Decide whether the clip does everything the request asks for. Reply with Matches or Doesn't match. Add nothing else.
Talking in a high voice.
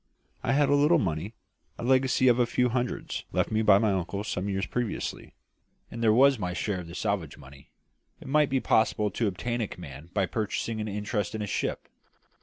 Doesn't match